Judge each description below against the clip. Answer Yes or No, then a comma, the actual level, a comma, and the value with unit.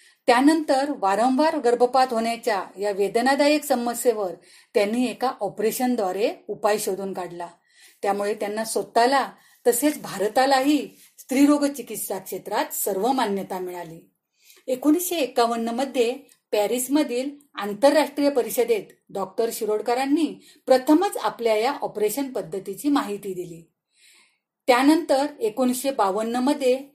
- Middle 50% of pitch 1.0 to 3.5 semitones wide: No, average, 5.3 semitones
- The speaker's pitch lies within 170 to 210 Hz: No, high, 240 Hz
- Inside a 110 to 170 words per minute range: No, average, 95 wpm